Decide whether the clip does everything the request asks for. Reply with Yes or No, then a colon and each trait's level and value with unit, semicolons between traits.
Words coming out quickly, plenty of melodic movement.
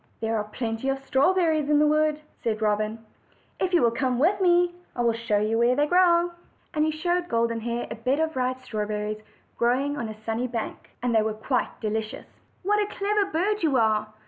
Yes: fast, 210 wpm; wide, 6.1 semitones